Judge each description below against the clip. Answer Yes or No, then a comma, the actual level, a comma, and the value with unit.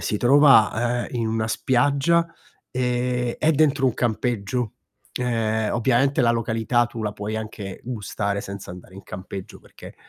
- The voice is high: No, low, 120 Hz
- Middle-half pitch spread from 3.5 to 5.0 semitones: No, average, 2.8 semitones